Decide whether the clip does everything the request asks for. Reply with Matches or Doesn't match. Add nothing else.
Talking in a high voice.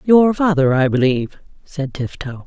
Doesn't match